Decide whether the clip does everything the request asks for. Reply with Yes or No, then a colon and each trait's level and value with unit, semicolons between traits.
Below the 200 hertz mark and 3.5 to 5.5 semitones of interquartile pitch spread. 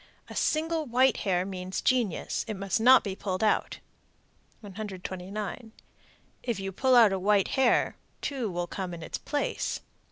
No: high, 205 Hz; average, 4.7 semitones